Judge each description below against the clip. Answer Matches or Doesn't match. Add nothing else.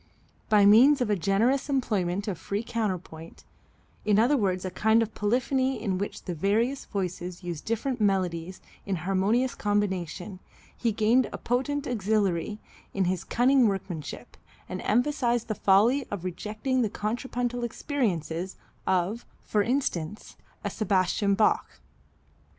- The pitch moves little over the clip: Doesn't match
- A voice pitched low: Doesn't match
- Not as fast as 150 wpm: Matches